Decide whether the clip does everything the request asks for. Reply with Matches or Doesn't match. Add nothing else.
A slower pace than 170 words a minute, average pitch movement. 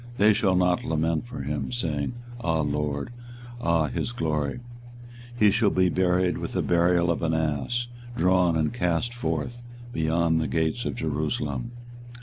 Matches